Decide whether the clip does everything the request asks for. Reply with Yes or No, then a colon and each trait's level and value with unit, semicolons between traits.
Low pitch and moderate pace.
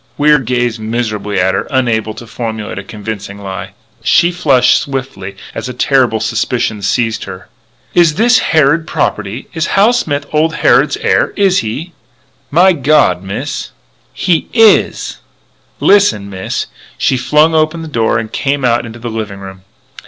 Yes: low, 125 Hz; average, 160 wpm